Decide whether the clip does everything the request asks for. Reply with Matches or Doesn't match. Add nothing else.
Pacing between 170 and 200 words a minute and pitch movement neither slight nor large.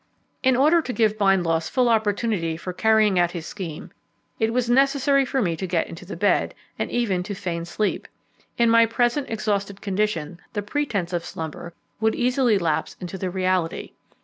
Matches